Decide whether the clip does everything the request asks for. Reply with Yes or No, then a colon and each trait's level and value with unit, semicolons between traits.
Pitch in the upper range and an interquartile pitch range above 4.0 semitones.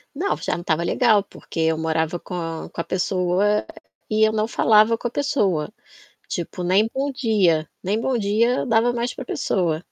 Yes: high, 210 Hz; average, 4.9 semitones